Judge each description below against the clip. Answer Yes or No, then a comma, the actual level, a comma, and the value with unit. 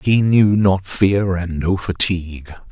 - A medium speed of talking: Yes, average, 155 wpm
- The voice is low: Yes, very low, 95 Hz